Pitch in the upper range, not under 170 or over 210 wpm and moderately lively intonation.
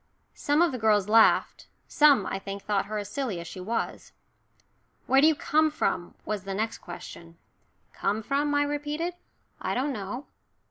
No: high, 225 Hz; average, 175 wpm; wide, 6.4 semitones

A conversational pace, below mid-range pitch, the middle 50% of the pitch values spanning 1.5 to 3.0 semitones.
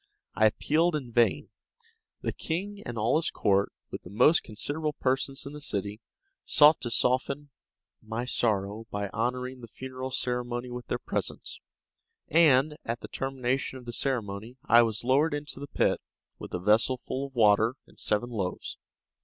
No: average, 165 wpm; low, 125 Hz; average, 3.7 semitones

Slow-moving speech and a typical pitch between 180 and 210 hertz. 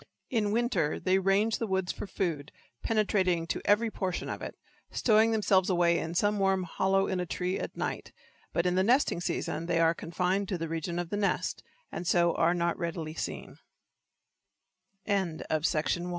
No: average, 170 wpm; medium, 185 Hz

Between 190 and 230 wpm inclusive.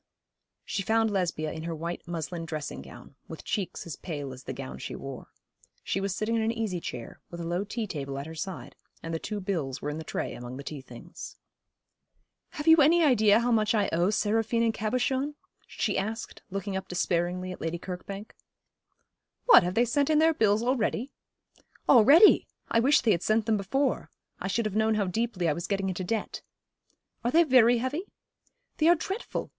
Yes: average, 200 wpm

